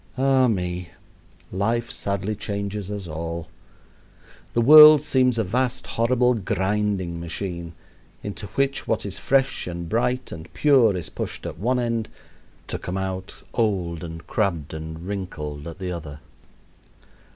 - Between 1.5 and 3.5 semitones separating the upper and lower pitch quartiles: No, wide, 5.6 semitones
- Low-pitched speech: Yes, low, 100 Hz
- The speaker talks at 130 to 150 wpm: Yes, average, 140 wpm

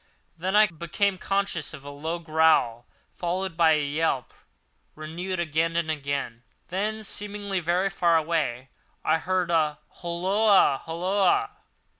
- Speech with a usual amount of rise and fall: Yes, average, 3.5 semitones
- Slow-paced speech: Yes, slow, 130 wpm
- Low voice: No, medium, 170 Hz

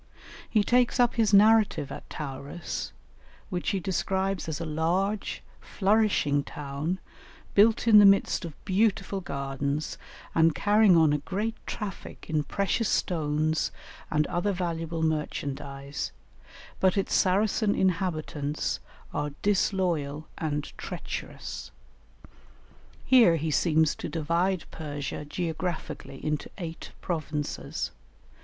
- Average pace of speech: No, slow, 110 wpm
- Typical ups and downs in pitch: Yes, average, 4.7 semitones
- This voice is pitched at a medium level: Yes, medium, 170 Hz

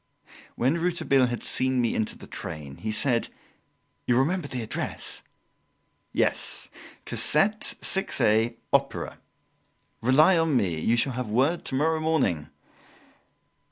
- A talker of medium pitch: No, low, 130 Hz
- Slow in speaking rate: Yes, slow, 120 wpm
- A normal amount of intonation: No, wide, 5.8 semitones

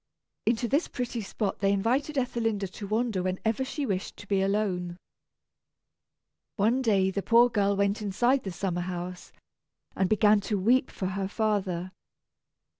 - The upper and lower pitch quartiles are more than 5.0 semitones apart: No, average, 3.3 semitones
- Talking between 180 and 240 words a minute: No, average, 155 wpm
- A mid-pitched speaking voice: No, high, 205 Hz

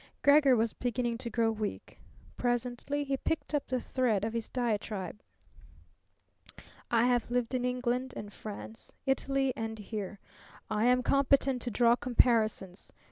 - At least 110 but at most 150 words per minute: Yes, slow, 135 wpm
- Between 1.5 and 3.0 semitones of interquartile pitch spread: Yes, narrow, 2.4 semitones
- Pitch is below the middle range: No, high, 240 Hz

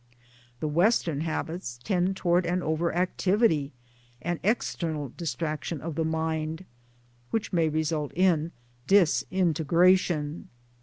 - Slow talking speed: Yes, slow, 105 wpm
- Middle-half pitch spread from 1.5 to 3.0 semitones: Yes, average, 2.7 semitones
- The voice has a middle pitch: Yes, medium, 165 Hz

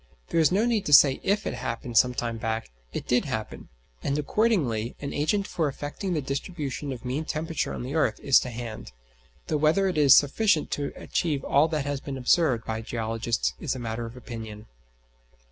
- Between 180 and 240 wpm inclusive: Yes, average, 195 wpm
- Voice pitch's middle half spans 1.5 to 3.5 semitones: No, average, 5.0 semitones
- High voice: No, medium, 140 Hz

